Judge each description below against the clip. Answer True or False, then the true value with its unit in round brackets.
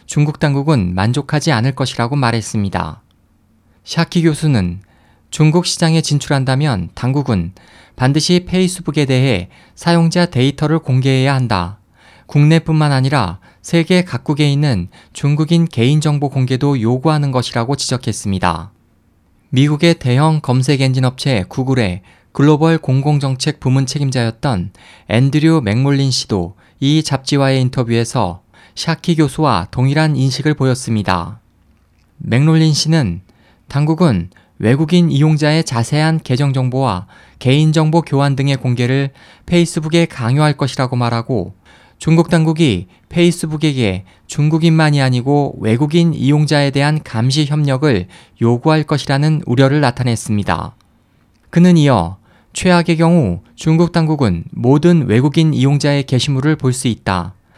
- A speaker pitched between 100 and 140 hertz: True (135 Hz)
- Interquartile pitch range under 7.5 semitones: True (5.4 semitones)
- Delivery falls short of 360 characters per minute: True (300 characters per minute)